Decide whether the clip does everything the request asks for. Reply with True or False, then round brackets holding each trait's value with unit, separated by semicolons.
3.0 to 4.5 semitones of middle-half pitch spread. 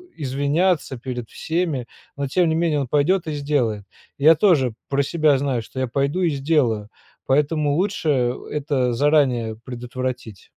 True (3.7 semitones)